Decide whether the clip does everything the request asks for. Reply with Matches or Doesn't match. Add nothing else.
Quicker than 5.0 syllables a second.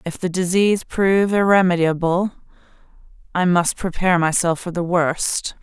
Doesn't match